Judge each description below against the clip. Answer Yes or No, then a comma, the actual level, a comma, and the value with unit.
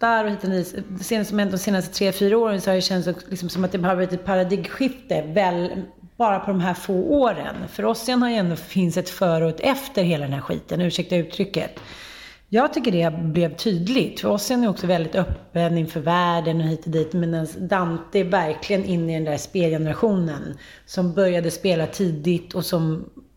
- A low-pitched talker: No, medium, 185 Hz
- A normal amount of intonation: Yes, average, 3.0 semitones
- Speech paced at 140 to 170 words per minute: No, fast, 195 wpm